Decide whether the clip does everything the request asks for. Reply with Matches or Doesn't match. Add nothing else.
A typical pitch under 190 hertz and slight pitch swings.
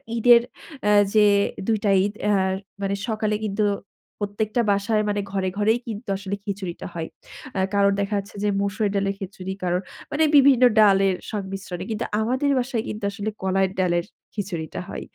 Doesn't match